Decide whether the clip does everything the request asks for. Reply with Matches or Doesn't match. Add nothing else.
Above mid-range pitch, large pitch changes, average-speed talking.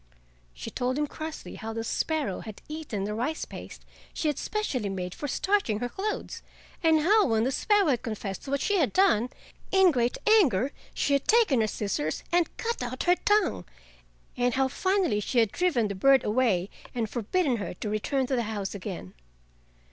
Matches